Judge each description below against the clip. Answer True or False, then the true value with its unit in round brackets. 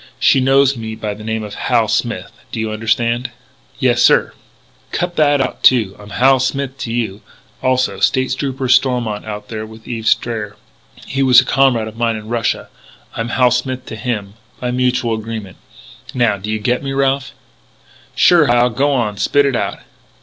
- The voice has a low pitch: True (120 Hz)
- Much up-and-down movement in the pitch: False (3.0 semitones)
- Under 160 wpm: False (185 wpm)